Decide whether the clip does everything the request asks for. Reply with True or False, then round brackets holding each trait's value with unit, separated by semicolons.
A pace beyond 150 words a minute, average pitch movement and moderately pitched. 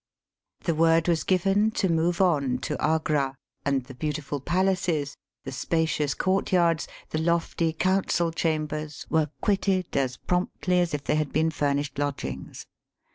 False (140 wpm; 3.4 semitones; 160 Hz)